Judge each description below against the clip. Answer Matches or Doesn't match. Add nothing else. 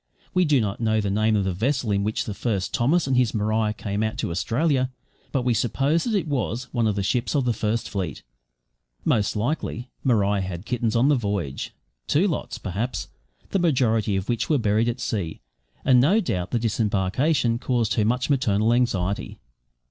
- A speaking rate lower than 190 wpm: Doesn't match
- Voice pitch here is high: Doesn't match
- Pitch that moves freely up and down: Doesn't match